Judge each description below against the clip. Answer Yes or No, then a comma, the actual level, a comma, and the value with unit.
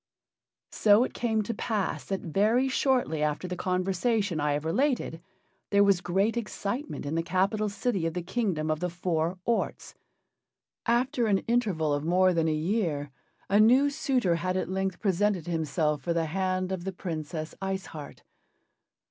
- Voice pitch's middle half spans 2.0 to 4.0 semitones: No, average, 4.7 semitones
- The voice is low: No, medium, 185 Hz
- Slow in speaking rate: No, average, 165 wpm